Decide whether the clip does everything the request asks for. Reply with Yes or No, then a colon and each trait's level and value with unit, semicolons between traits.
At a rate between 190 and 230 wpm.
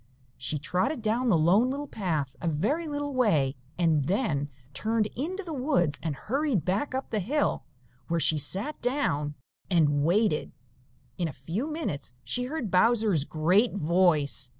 No: average, 155 wpm